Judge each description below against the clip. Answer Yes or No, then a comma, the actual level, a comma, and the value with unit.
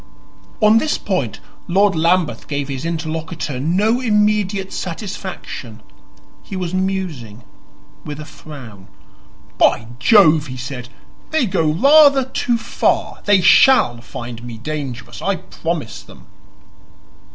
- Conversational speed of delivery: No, slow, 120 wpm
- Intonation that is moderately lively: No, wide, 7.2 semitones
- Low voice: No, medium, 165 Hz